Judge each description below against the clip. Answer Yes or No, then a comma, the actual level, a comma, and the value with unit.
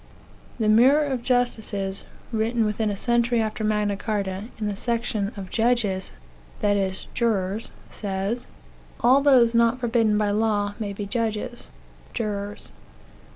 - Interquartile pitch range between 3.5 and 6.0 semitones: No, narrow, 2.6 semitones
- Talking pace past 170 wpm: No, average, 150 wpm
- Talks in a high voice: Yes, high, 215 Hz